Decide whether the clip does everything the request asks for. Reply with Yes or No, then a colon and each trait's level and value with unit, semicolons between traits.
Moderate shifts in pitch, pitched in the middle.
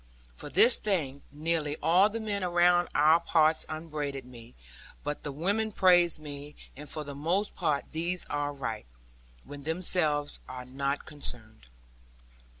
Yes: average, 3.7 semitones; medium, 155 Hz